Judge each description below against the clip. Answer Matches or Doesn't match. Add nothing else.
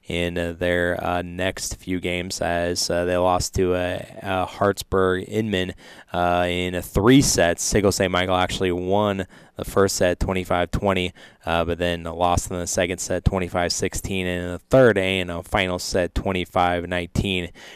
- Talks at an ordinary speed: Matches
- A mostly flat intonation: Matches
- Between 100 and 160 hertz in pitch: Doesn't match